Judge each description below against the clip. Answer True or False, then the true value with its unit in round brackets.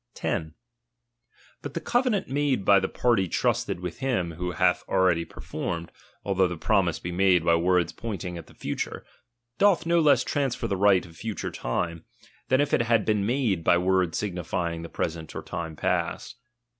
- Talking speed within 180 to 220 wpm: True (185 wpm)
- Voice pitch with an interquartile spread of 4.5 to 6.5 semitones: True (5.5 semitones)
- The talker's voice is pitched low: True (95 Hz)